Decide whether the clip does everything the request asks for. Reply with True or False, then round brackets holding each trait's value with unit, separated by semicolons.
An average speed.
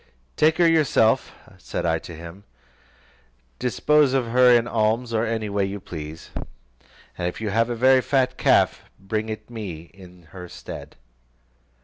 True (155 wpm)